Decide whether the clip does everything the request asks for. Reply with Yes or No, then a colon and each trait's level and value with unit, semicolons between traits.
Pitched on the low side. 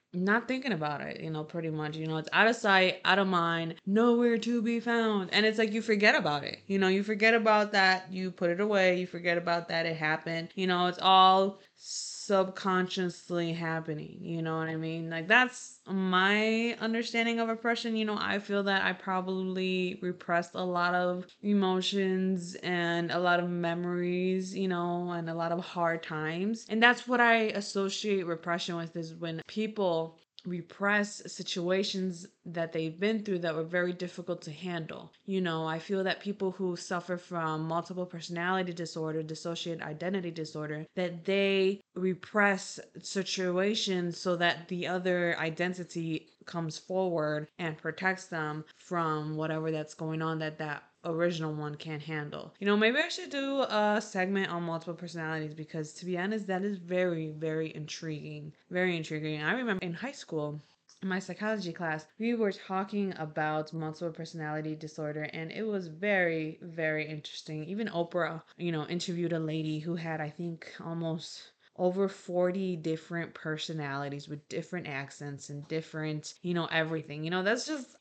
No: medium, 175 Hz